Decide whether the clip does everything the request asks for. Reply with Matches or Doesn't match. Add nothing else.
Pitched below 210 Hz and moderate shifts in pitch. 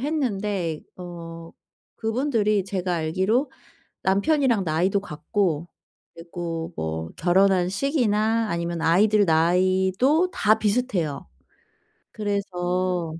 Matches